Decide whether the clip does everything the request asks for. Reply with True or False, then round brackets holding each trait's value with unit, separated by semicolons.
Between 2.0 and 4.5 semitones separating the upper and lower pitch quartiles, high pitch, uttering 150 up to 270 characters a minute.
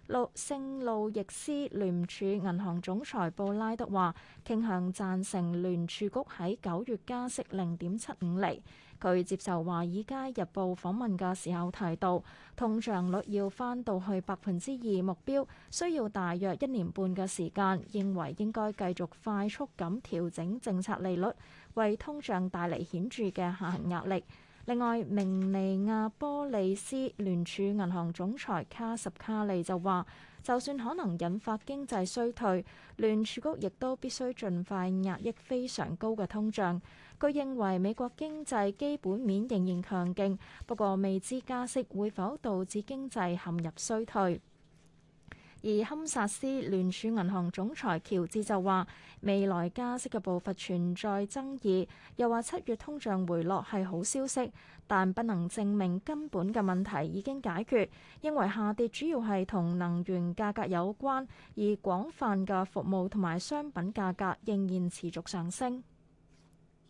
True (4.1 semitones; 200 Hz; 230 characters per minute)